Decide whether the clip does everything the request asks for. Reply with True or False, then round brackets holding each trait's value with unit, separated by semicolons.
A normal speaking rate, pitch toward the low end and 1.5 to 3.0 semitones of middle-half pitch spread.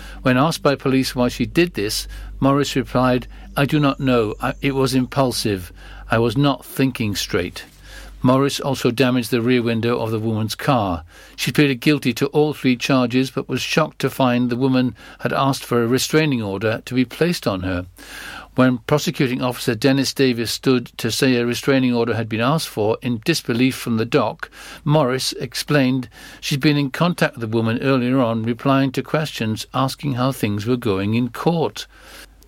True (185 wpm; 130 Hz; 2.7 semitones)